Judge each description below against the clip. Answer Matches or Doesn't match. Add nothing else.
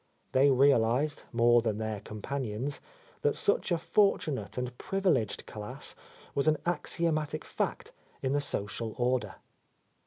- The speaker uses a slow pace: Matches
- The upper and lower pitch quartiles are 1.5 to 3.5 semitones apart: Doesn't match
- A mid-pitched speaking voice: Doesn't match